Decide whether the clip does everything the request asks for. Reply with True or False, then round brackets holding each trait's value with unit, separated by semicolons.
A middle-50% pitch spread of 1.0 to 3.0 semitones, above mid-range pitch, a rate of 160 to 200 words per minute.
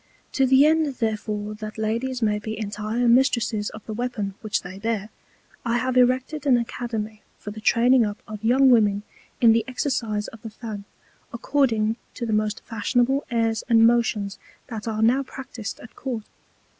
True (2.6 semitones; 225 Hz; 170 wpm)